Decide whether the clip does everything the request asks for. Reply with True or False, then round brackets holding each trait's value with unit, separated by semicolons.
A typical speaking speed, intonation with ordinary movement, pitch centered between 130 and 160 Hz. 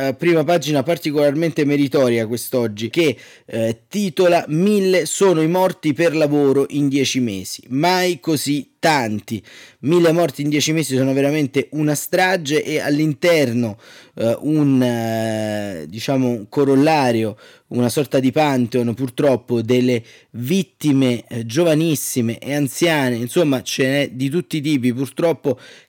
True (130 wpm; 4.4 semitones; 140 Hz)